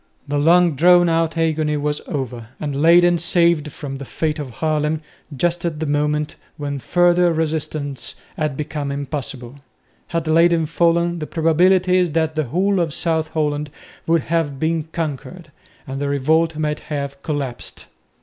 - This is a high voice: No, medium, 155 Hz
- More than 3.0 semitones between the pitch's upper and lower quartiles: No, narrow, 2.5 semitones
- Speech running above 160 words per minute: No, average, 155 wpm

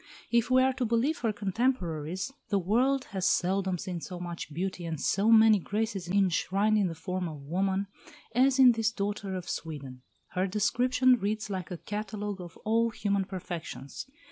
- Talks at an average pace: Yes, average, 170 wpm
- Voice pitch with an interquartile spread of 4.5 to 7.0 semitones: No, average, 3.9 semitones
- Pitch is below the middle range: No, high, 200 Hz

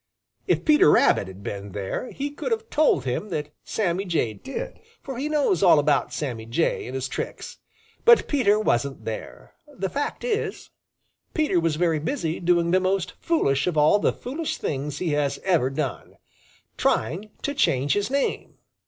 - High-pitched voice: No, medium, 170 Hz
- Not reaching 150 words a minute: No, average, 170 wpm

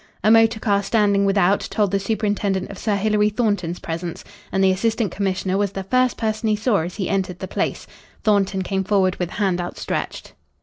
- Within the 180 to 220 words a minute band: Yes, average, 190 wpm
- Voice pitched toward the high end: Yes, high, 200 Hz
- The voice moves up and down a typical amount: No, narrow, 2.1 semitones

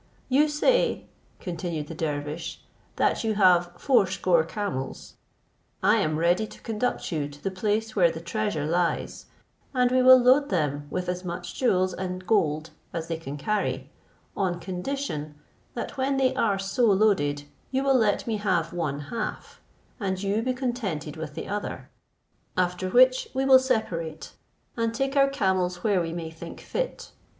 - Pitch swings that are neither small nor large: No, wide, 5.7 semitones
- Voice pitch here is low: No, medium, 185 Hz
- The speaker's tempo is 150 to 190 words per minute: Yes, average, 160 wpm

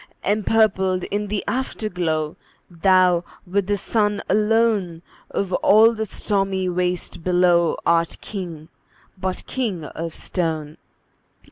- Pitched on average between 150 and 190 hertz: Yes, medium, 185 Hz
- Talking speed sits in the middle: No, slow, 110 wpm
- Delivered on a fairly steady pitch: No, average, 3.3 semitones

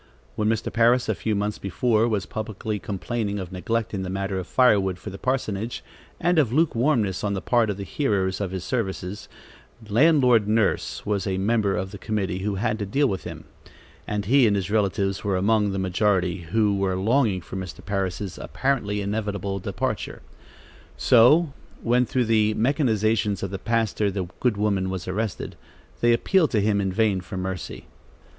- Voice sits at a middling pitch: No, low, 105 Hz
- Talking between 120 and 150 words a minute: No, average, 180 wpm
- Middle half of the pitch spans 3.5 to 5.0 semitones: No, average, 3.0 semitones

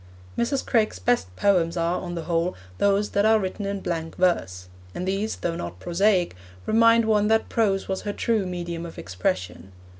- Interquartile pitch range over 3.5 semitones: Yes, average, 3.9 semitones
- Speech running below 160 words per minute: No, average, 180 wpm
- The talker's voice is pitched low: No, medium, 185 Hz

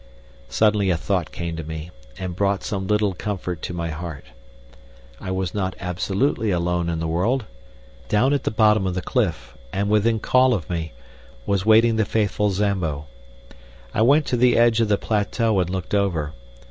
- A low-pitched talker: Yes, low, 100 Hz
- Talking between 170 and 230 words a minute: Yes, average, 180 wpm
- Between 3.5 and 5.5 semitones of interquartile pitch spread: Yes, average, 3.8 semitones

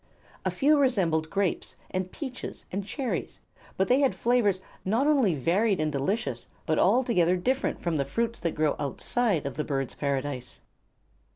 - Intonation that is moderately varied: No, wide, 7.9 semitones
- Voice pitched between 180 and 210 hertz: Yes, medium, 185 Hz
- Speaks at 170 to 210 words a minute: No, average, 160 wpm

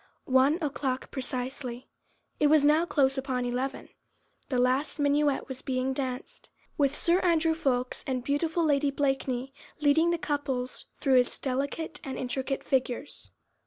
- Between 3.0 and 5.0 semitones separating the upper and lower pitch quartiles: No, narrow, 2.4 semitones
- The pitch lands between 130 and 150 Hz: No, very high, 270 Hz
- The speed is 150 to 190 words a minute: No, average, 140 wpm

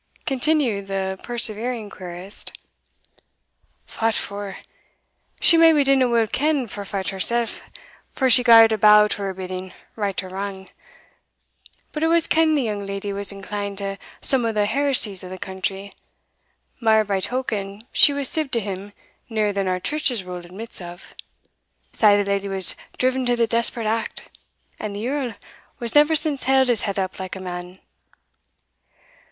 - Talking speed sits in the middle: Yes, average, 160 wpm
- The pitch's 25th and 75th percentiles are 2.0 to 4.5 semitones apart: Yes, average, 4.2 semitones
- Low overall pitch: No, high, 210 Hz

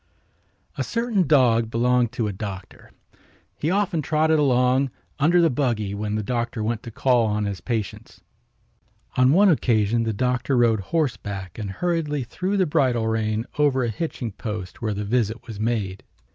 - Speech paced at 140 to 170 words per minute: Yes, average, 165 wpm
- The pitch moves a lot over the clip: No, average, 5.0 semitones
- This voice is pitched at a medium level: No, low, 120 Hz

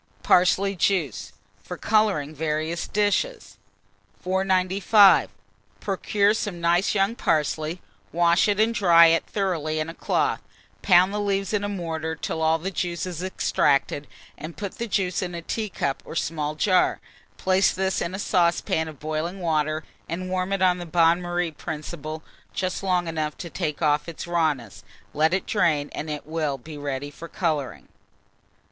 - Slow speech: No, average, 160 wpm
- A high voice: No, medium, 170 Hz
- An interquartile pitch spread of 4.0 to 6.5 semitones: No, average, 3.4 semitones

